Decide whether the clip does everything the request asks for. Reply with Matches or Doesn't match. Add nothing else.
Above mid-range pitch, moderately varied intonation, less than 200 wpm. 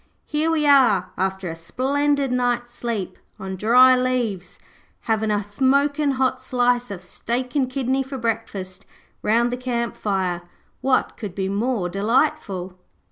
Matches